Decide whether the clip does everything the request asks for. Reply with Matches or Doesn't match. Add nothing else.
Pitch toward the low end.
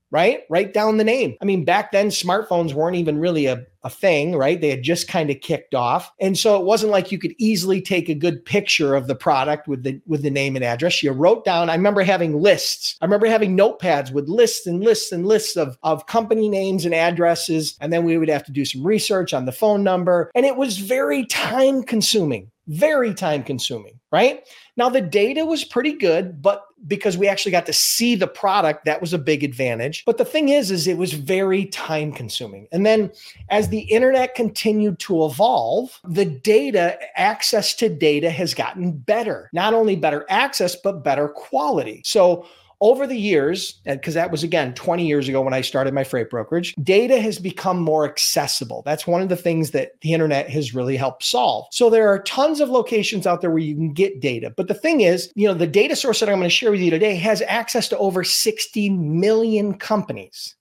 Doesn't match